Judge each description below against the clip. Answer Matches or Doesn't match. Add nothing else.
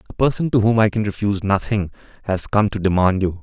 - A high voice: Doesn't match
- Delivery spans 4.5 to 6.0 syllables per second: Doesn't match